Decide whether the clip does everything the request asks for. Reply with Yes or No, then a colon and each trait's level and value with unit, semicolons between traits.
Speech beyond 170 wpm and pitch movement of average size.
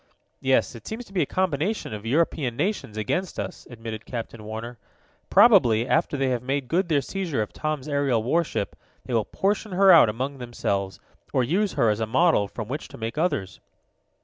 No: average, 190 wpm; wide, 6.7 semitones